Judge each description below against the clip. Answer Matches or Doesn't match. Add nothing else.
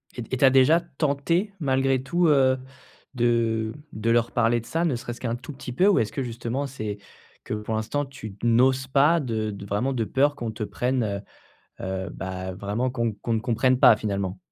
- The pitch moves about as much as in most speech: Matches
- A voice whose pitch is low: Matches